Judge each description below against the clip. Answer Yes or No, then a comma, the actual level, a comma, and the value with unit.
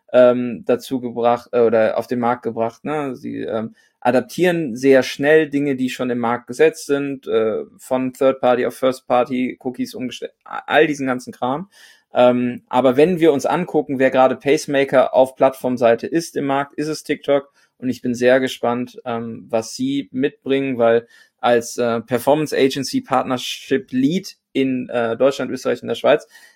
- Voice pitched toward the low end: Yes, low, 130 Hz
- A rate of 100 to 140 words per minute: No, average, 160 wpm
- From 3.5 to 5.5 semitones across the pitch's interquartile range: No, average, 2.8 semitones